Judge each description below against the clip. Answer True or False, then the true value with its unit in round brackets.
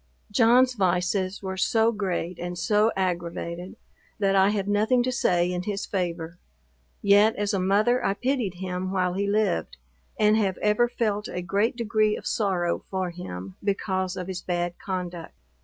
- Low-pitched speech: False (195 Hz)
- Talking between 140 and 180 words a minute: True (165 wpm)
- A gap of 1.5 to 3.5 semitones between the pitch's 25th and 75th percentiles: True (2.9 semitones)